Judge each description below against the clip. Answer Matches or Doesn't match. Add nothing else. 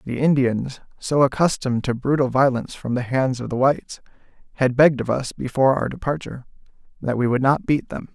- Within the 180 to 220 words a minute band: Matches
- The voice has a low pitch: Matches